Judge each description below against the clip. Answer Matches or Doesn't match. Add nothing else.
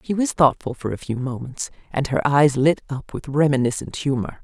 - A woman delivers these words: Matches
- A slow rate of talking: Doesn't match